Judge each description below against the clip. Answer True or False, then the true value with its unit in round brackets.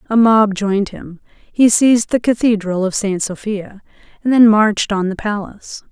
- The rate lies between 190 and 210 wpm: False (170 wpm)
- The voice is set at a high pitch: True (210 Hz)